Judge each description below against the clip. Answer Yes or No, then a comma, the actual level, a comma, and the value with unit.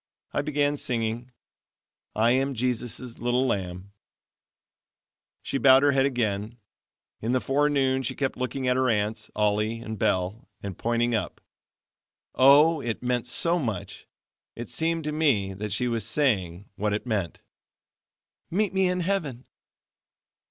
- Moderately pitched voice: No, low, 125 Hz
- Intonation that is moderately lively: Yes, average, 4.3 semitones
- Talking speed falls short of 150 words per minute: Yes, average, 140 wpm